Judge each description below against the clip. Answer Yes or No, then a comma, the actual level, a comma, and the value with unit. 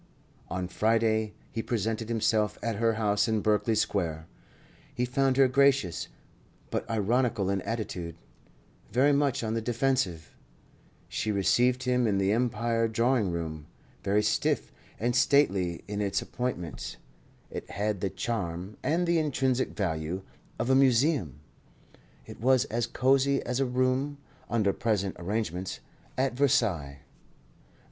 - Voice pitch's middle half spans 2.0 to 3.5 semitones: No, average, 4.4 semitones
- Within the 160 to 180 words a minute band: No, slow, 135 wpm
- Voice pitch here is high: No, low, 115 Hz